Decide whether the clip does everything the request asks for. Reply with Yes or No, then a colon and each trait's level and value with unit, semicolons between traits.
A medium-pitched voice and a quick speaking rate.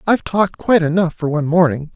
Yes: medium, 170 Hz; fast, 215 wpm